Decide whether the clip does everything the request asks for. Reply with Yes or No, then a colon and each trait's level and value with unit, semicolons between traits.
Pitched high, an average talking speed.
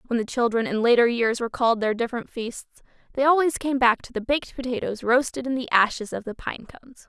No: high, 240 Hz; fast, 220 wpm